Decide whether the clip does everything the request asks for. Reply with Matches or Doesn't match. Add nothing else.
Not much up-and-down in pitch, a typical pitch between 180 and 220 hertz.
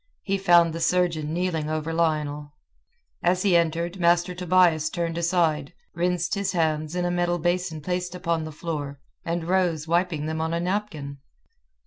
Doesn't match